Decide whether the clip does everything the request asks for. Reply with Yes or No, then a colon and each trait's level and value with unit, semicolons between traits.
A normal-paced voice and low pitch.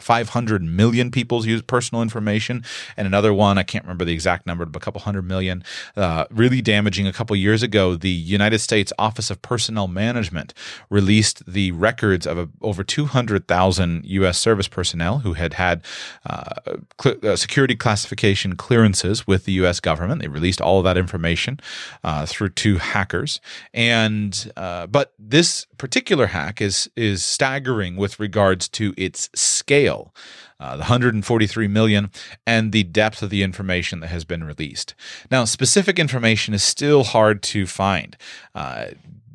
Yes: average, 160 wpm; low, 105 Hz